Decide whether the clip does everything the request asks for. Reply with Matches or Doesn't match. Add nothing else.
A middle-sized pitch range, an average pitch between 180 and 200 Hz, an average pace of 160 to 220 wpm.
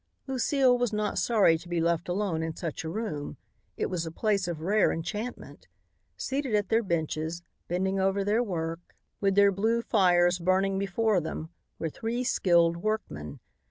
Matches